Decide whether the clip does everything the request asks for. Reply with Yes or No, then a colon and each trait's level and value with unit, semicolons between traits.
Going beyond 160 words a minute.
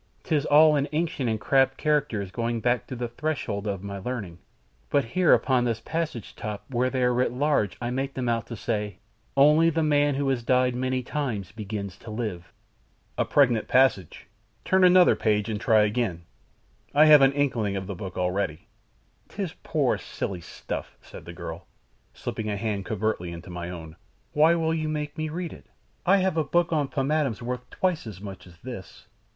Yes: average, 190 wpm